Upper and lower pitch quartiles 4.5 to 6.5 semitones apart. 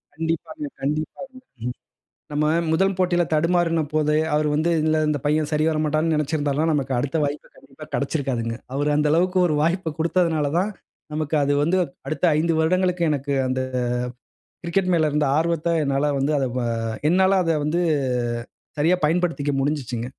No: narrow, 2.6 semitones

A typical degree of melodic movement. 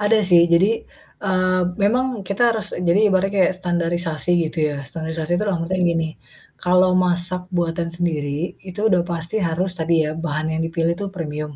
No: narrow, 2.1 semitones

